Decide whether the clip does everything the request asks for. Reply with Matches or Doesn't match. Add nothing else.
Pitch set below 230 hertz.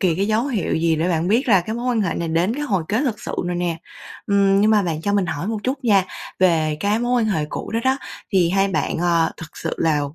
Matches